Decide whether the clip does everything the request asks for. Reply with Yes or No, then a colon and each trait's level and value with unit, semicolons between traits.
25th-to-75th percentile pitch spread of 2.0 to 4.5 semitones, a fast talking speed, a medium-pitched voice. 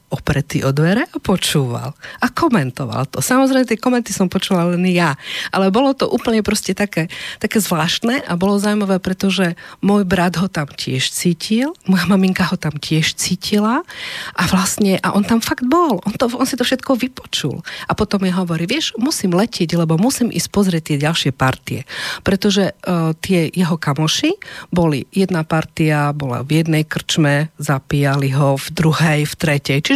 No: wide, 5.6 semitones; fast, 170 wpm; medium, 180 Hz